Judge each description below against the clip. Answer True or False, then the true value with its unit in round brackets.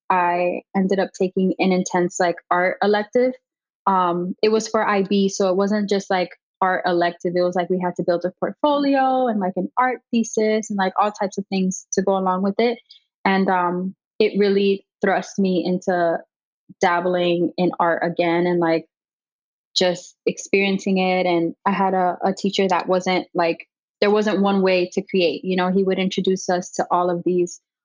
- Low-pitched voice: False (185 Hz)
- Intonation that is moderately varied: False (1.9 semitones)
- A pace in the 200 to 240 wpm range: False (185 wpm)